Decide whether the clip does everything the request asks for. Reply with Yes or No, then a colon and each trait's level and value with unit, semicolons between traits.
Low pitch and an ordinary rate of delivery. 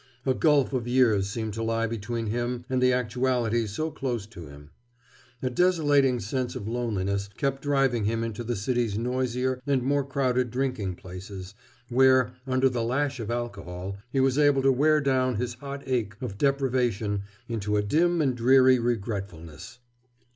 Yes: low, 120 Hz; average, 165 wpm